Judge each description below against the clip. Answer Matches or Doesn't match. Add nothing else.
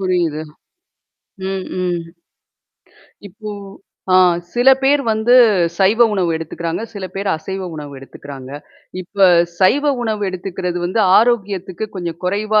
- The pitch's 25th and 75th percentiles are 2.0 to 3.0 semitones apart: Doesn't match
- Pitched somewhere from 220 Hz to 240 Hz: Doesn't match